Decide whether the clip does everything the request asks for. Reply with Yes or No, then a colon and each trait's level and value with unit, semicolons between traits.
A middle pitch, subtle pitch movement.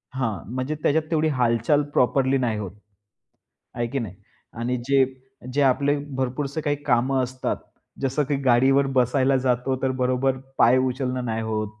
No: low, 130 Hz; narrow, 2.0 semitones